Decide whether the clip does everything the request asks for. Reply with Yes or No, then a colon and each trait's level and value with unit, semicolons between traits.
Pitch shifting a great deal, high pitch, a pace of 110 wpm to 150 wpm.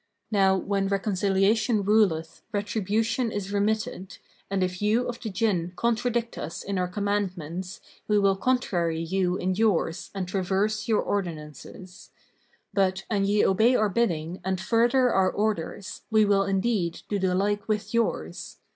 No: narrow, 2.6 semitones; high, 200 Hz; average, 145 wpm